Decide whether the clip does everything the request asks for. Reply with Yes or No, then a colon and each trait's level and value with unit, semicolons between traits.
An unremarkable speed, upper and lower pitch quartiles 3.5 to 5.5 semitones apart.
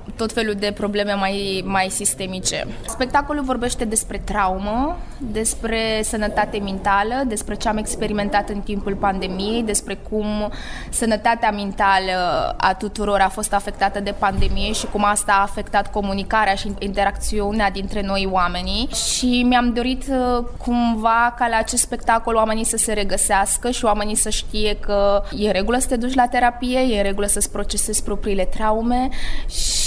No: average, 150 wpm; narrow, 2.5 semitones